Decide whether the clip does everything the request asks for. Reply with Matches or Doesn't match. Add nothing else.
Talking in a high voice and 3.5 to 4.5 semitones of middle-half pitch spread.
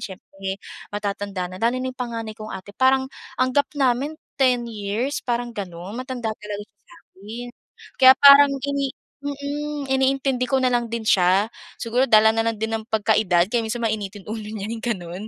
Matches